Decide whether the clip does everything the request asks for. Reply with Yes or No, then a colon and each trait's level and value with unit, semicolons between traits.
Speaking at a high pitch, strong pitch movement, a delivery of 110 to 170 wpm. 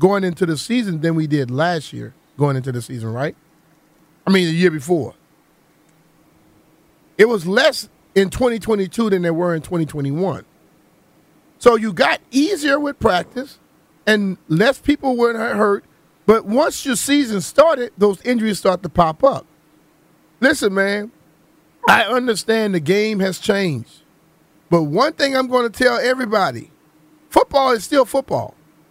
Yes: high, 195 Hz; wide, 6.9 semitones; average, 145 wpm